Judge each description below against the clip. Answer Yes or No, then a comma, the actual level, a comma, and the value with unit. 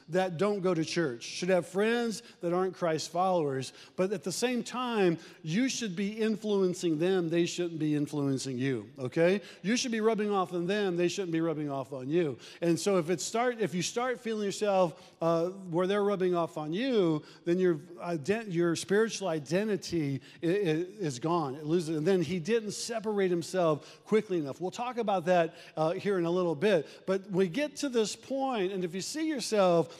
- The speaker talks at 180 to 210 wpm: Yes, average, 195 wpm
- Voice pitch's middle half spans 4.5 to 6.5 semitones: No, average, 3.5 semitones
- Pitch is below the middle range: No, medium, 180 Hz